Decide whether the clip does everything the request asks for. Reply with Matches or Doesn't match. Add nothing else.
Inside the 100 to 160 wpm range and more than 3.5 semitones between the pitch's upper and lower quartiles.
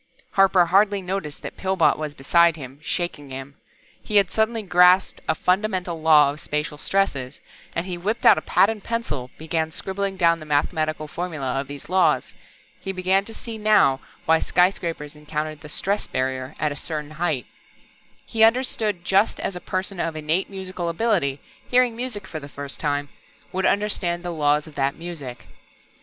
Doesn't match